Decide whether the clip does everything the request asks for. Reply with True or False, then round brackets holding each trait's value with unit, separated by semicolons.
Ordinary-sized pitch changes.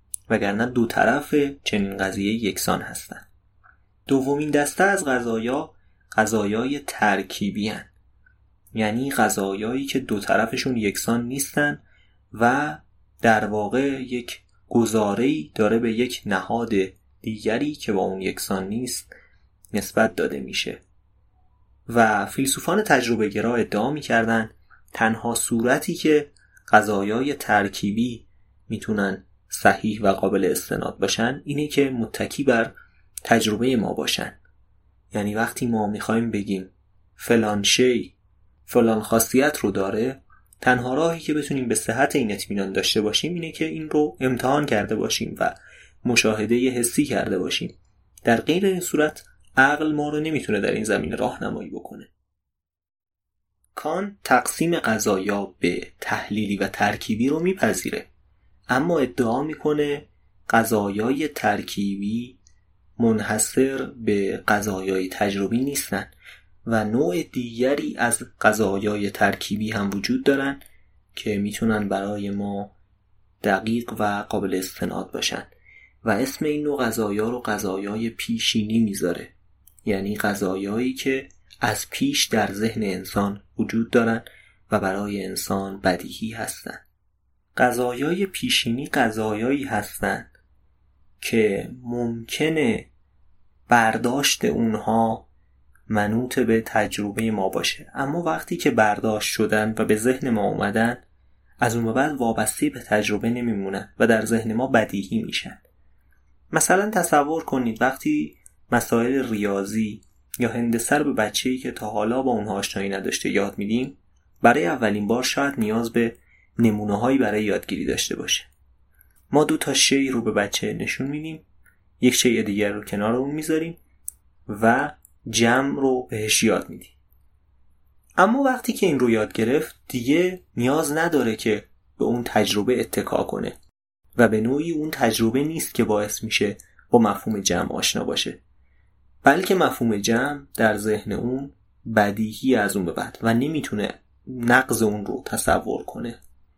True (4.4 semitones)